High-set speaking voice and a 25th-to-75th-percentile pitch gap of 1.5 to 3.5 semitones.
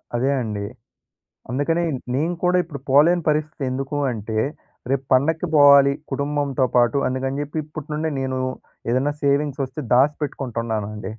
No: medium, 140 Hz; narrow, 2.6 semitones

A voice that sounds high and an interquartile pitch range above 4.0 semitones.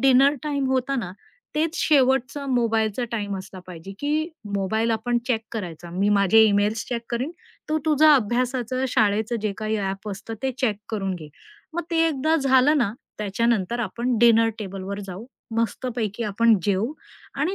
Yes: high, 230 Hz; average, 4.5 semitones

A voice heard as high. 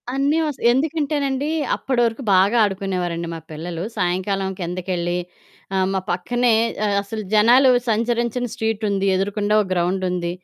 Yes: high, 205 Hz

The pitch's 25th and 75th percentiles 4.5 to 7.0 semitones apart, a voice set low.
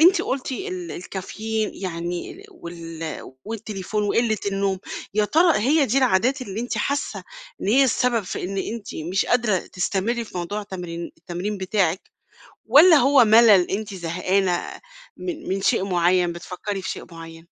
No: average, 4.9 semitones; high, 200 Hz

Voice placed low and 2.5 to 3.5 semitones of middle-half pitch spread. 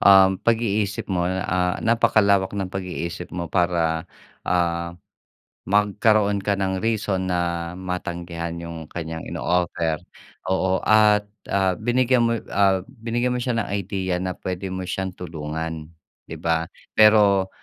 Yes: very low, 95 Hz; average, 3.1 semitones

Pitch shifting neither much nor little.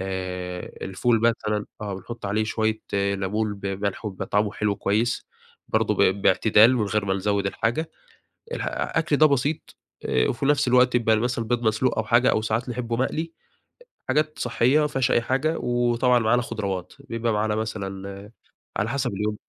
Yes: average, 3.3 semitones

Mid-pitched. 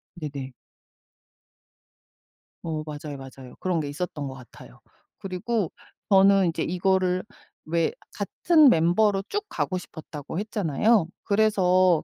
Yes: medium, 180 Hz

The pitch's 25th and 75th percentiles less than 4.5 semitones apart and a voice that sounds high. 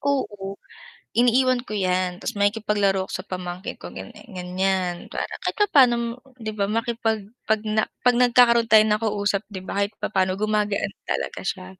Yes: average, 3.3 semitones; high, 210 Hz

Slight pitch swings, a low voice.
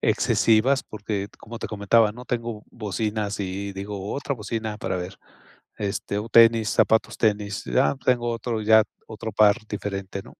Yes: narrow, 2.1 semitones; low, 110 Hz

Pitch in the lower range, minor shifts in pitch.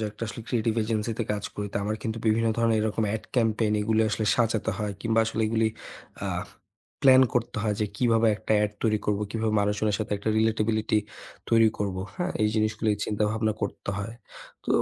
Yes: low, 110 Hz; narrow, 1.2 semitones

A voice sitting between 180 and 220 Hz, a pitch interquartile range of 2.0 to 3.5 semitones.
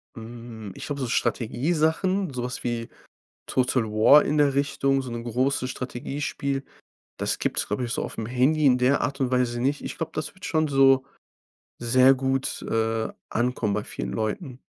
No: low, 130 Hz; average, 2.8 semitones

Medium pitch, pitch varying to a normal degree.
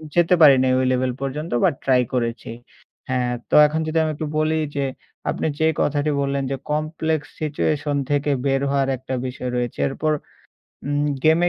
Yes: medium, 145 Hz; average, 3.0 semitones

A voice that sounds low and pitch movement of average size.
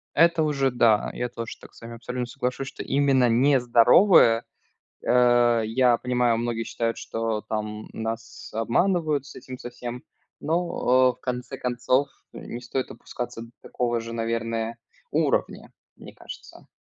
No: low, 120 Hz; narrow, 2.0 semitones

